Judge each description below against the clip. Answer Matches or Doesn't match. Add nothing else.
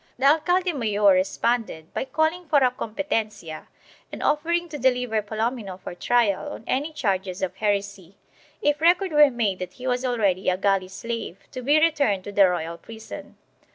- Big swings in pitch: Matches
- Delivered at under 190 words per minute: Matches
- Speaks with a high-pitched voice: Matches